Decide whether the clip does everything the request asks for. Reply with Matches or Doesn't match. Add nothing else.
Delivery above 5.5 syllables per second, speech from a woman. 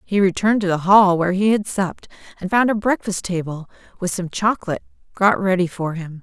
Matches